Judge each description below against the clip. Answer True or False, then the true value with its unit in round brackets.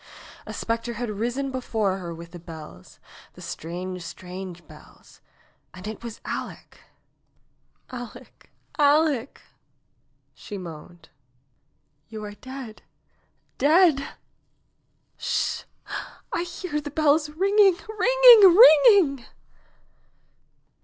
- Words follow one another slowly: True (110 wpm)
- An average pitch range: False (8.7 semitones)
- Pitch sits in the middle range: False (245 Hz)